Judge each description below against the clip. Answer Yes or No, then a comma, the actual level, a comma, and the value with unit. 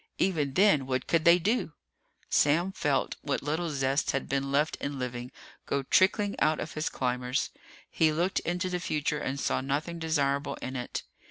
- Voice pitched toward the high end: No, medium, 150 Hz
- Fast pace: No, average, 175 wpm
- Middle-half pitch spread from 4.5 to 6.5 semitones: No, average, 3.8 semitones